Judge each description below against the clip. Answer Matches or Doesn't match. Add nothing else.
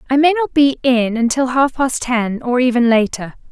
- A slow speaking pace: Doesn't match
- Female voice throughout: Matches